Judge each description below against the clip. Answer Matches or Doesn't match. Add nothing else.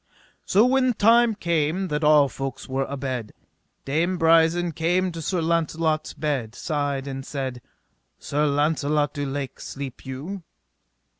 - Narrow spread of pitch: Doesn't match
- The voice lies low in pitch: Doesn't match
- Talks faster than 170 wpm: Doesn't match